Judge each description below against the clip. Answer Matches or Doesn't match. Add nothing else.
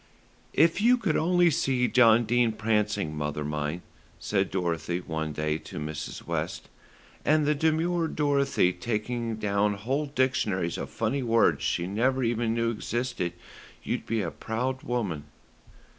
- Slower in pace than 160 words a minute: Matches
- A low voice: Matches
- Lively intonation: Matches